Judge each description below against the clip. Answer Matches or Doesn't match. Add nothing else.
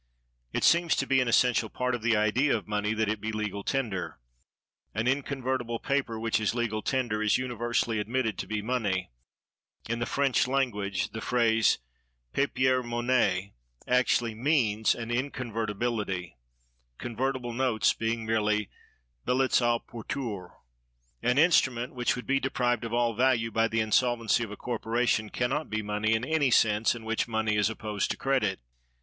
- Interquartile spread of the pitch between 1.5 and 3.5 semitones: Matches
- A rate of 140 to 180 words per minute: Matches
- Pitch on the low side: Matches